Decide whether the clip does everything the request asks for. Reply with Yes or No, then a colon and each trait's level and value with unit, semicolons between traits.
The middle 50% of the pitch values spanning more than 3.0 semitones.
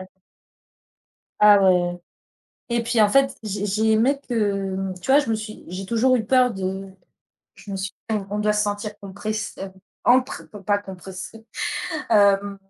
No: narrow, 2.5 semitones